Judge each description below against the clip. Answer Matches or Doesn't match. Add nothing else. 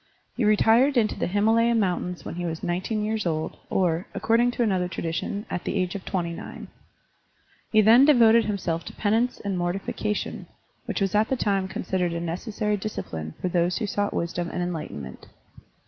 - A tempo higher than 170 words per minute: Matches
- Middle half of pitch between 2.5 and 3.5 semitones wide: Doesn't match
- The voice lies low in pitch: Doesn't match